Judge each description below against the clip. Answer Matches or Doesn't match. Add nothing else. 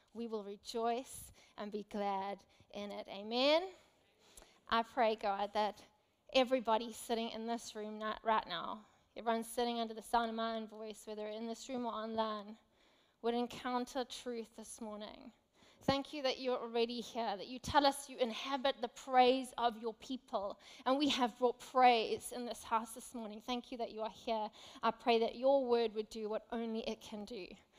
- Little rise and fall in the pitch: Matches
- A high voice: Matches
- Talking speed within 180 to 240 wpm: Matches